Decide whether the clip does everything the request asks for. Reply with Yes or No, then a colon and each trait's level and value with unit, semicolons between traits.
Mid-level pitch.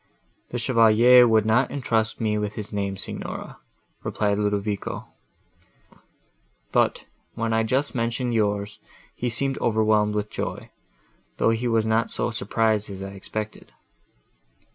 No: low, 110 Hz